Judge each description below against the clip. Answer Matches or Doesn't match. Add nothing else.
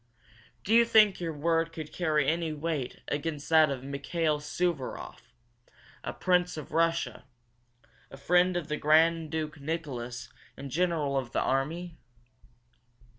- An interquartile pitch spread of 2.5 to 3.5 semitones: Matches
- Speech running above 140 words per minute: Doesn't match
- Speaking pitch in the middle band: Matches